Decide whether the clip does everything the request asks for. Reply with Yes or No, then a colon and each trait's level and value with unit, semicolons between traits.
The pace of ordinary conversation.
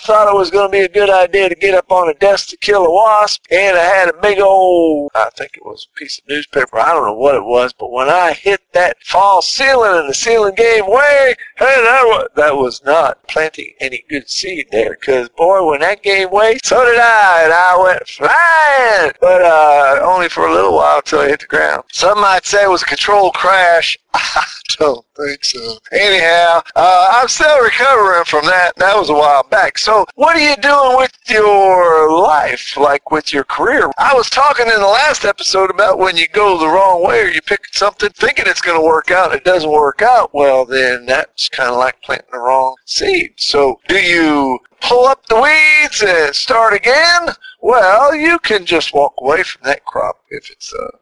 No: fast, 215 wpm